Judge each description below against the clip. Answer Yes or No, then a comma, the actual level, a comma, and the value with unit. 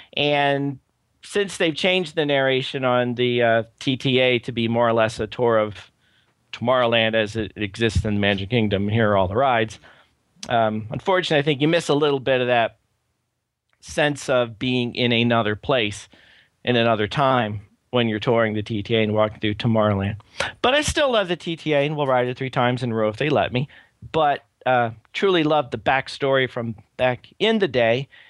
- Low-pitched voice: Yes, low, 120 Hz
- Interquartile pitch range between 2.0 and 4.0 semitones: Yes, average, 3.7 semitones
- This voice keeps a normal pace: Yes, average, 190 wpm